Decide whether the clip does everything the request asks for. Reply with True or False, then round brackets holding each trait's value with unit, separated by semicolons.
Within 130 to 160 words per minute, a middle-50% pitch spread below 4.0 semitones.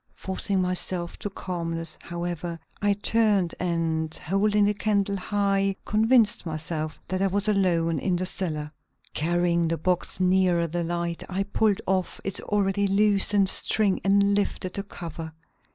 True (145 wpm; 2.8 semitones)